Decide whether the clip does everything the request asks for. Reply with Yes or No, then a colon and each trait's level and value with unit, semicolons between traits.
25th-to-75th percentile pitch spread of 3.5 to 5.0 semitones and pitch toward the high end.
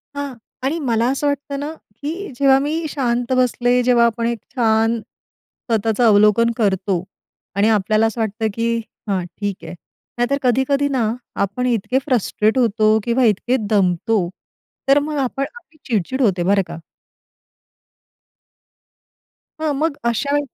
Yes: average, 4.1 semitones; high, 235 Hz